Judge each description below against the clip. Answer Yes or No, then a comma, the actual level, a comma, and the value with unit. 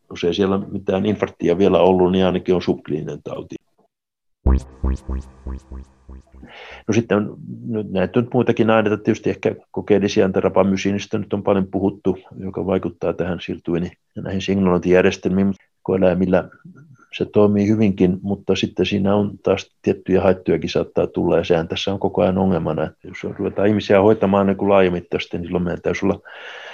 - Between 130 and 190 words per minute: Yes, average, 145 wpm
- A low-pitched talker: Yes, very low, 95 Hz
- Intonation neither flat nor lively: No, narrow, 2.2 semitones